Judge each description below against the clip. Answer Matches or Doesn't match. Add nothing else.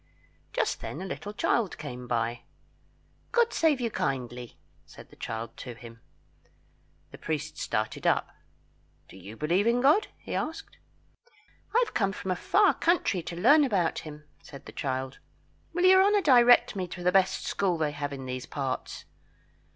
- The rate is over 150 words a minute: Matches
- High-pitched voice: Doesn't match